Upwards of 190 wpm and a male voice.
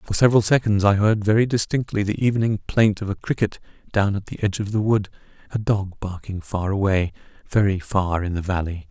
Yes: average, 200 wpm; male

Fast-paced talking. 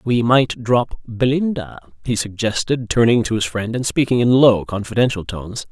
No: average, 170 wpm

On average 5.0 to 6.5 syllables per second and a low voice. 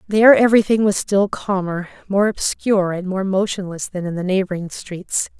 No: 5.2 syllables/s; high, 190 Hz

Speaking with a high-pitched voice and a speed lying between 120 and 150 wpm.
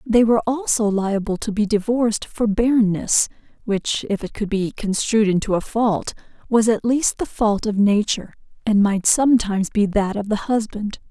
No: high, 215 Hz; average, 180 wpm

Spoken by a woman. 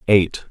No: male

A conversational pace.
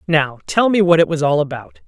No: fast, 255 wpm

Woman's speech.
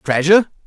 No: male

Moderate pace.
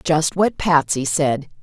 Yes: average, 150 wpm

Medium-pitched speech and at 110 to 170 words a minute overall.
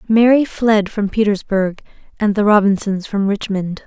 No: high, 205 Hz; average, 140 wpm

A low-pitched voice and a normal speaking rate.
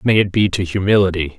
No: very low, 95 Hz; fast, 215 wpm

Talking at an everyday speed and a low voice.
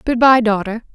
No: average, 190 wpm; high, 230 Hz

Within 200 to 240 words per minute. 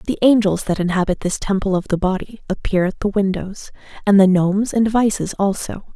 No: average, 190 wpm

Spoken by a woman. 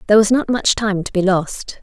Yes: female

